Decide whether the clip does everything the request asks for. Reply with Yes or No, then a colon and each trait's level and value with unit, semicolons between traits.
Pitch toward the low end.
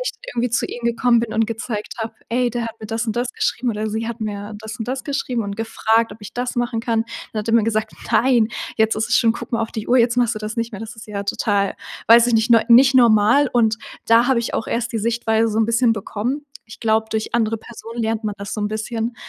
No: high, 225 Hz